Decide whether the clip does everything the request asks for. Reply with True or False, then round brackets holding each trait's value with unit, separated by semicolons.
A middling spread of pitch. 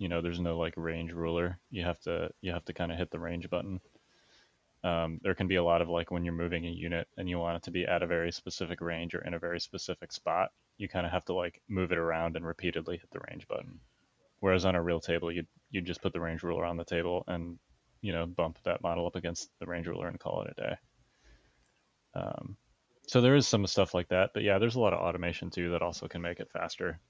False (1.4 semitones)